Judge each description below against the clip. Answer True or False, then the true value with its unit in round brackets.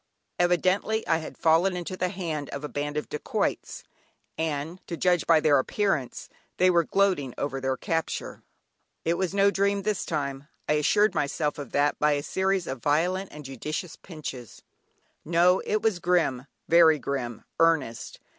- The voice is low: False (160 Hz)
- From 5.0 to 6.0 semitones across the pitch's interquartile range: False (4.1 semitones)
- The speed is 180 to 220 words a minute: False (165 wpm)